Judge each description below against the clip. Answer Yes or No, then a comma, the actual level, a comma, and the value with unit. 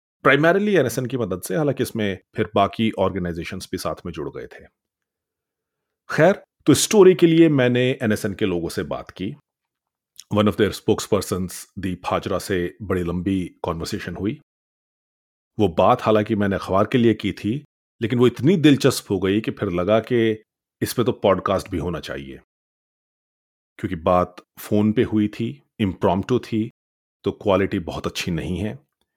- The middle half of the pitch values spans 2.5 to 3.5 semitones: No, average, 4.7 semitones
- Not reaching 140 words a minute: No, fast, 165 wpm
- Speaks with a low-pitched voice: Yes, low, 105 Hz